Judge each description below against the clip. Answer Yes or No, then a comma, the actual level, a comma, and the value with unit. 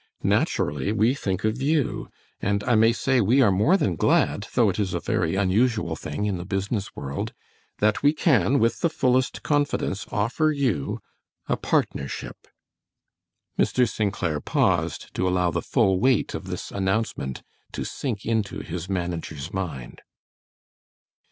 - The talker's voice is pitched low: Yes, low, 105 Hz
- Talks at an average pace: Yes, average, 150 wpm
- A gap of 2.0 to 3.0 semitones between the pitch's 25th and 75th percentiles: No, average, 5.2 semitones